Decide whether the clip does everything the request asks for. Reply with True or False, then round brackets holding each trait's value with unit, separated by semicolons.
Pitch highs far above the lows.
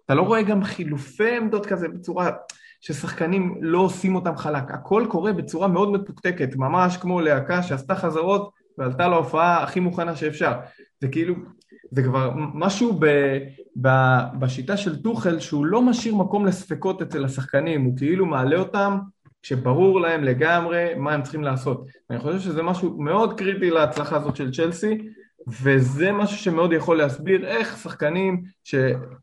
False (4.8 semitones)